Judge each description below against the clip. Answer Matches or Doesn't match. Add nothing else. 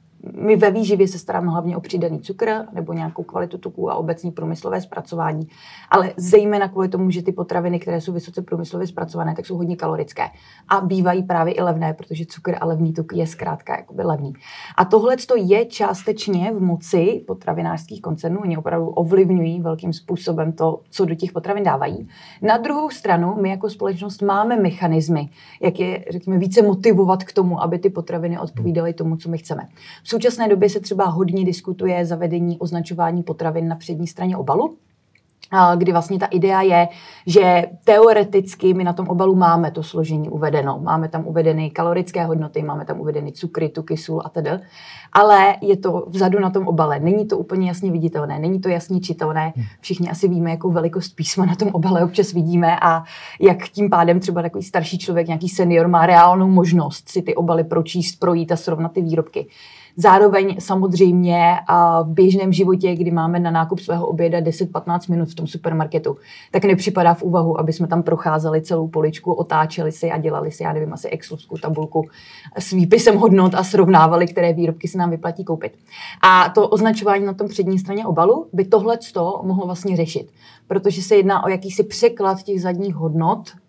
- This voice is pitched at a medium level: Matches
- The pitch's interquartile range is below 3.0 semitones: Matches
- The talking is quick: Matches